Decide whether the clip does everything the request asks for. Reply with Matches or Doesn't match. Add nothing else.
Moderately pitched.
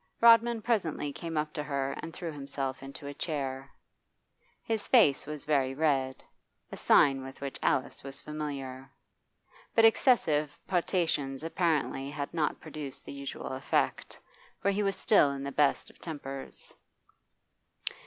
Matches